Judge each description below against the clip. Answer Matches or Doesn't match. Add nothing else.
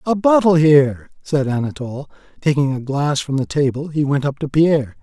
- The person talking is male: Matches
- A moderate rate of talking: Matches